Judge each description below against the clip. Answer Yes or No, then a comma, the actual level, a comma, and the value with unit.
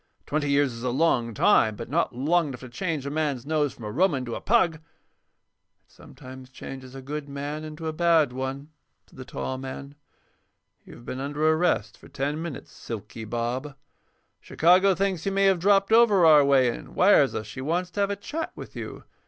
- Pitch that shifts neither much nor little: Yes, average, 4.7 semitones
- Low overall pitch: No, medium, 145 Hz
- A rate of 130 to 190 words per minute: No, average, 200 wpm